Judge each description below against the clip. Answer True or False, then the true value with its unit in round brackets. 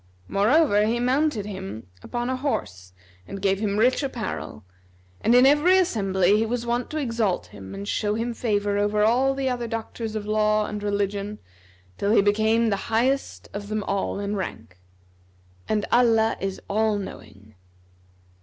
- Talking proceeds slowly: False (165 wpm)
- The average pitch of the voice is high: True (215 Hz)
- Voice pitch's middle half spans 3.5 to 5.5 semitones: False (3.1 semitones)